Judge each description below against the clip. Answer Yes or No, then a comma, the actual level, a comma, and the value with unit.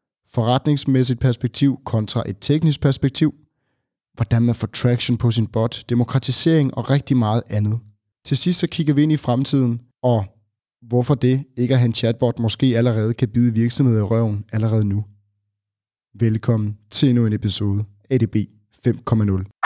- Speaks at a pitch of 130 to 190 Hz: No, low, 120 Hz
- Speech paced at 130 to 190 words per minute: Yes, average, 155 wpm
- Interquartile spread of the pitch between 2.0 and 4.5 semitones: Yes, average, 3.3 semitones